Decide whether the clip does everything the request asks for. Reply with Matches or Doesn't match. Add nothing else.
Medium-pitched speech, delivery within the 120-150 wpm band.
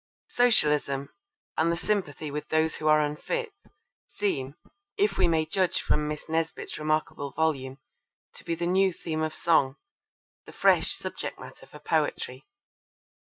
Matches